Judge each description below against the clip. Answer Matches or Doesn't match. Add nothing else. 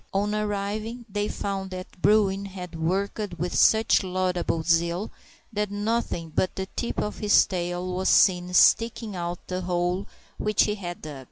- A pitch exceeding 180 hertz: Matches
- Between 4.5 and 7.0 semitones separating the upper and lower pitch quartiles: Doesn't match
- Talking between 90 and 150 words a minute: Doesn't match